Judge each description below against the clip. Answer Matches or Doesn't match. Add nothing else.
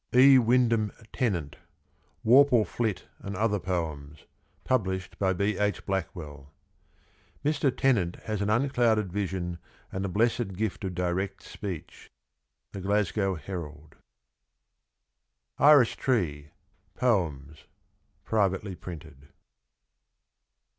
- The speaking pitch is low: Matches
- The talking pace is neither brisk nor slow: Doesn't match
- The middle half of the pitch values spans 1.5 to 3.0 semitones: Doesn't match